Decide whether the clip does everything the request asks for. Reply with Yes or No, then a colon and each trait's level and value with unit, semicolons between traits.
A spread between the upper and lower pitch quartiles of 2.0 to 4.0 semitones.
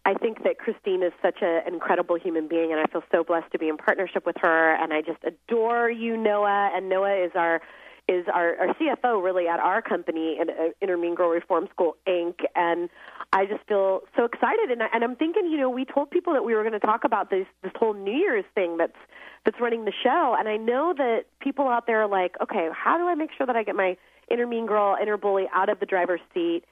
No: wide, 5.4 semitones